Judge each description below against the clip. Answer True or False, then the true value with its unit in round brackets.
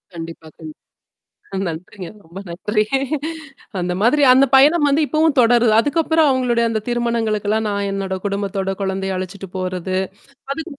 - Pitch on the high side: True (210 Hz)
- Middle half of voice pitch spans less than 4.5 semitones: False (5.2 semitones)